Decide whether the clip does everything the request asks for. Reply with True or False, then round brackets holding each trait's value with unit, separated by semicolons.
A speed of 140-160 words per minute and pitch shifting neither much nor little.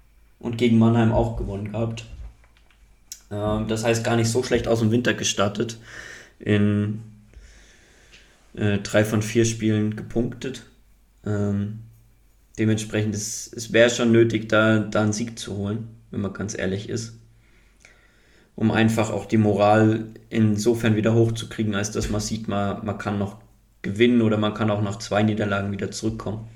False (145 wpm; 1.5 semitones)